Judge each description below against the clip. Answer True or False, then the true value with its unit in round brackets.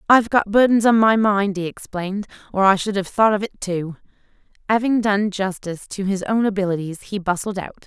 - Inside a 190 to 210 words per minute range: True (200 wpm)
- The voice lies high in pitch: True (200 Hz)